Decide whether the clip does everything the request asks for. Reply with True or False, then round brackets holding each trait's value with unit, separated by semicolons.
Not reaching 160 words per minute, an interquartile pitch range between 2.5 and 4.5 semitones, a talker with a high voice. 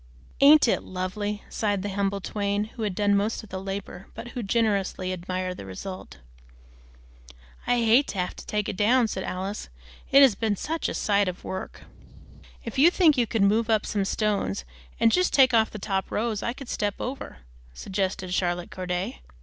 False (190 wpm; 3.3 semitones; 205 Hz)